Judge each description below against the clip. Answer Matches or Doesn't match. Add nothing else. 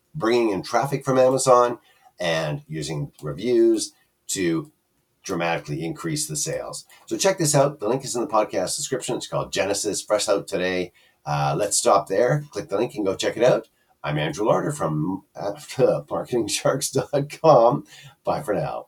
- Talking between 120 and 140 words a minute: Doesn't match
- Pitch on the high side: Doesn't match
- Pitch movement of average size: Doesn't match